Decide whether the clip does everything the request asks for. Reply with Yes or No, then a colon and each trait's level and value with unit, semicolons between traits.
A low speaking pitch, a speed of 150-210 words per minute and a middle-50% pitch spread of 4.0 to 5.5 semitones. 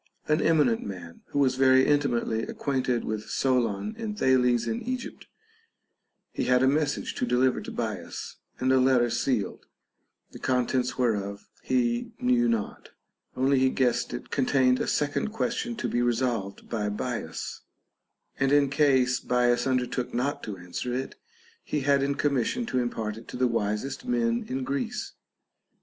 No: low, 130 Hz; average, 160 wpm; average, 2.8 semitones